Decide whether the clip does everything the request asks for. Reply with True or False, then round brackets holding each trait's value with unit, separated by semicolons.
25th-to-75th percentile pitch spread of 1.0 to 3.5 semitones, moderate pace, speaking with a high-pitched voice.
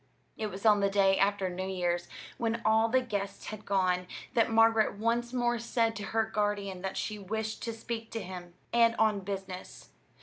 True (2.8 semitones; 190 wpm; 210 Hz)